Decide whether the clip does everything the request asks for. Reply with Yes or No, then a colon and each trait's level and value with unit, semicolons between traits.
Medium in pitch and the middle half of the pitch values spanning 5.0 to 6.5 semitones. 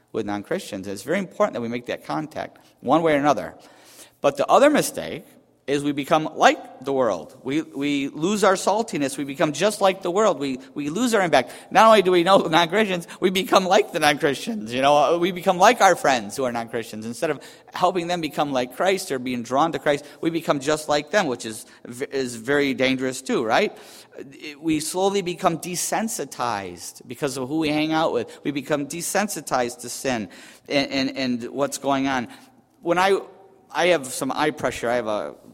Yes: medium, 150 Hz; average, 5.3 semitones